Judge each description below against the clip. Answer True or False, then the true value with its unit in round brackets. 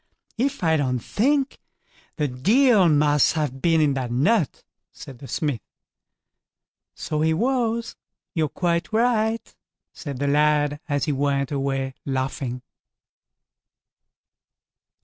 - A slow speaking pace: True (115 wpm)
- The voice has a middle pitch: True (150 Hz)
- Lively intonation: True (7.2 semitones)